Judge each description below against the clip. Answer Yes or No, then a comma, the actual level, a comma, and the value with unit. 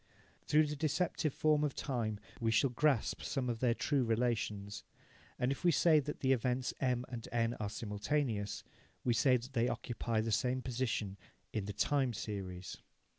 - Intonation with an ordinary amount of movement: Yes, average, 3.7 semitones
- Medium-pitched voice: No, low, 125 Hz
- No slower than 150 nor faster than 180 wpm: Yes, average, 170 wpm